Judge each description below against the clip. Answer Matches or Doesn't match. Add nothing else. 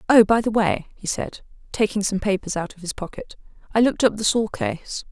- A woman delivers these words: Matches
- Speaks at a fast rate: Matches